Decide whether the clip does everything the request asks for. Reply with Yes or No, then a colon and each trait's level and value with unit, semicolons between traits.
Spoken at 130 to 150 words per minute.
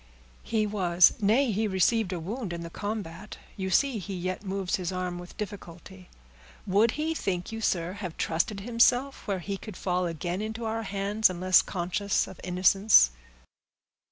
No: average, 165 wpm